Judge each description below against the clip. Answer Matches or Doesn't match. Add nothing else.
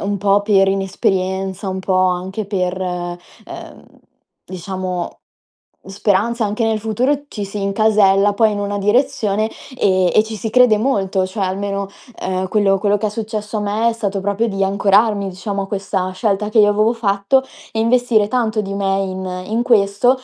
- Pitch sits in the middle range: Doesn't match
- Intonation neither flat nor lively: Doesn't match